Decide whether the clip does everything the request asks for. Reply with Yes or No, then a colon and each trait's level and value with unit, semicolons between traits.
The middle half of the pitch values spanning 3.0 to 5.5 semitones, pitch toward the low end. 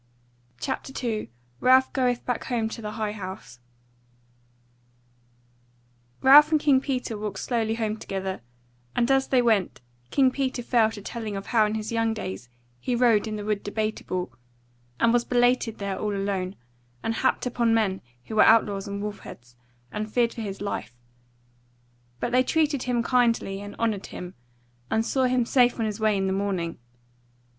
No: average, 3.4 semitones; high, 220 Hz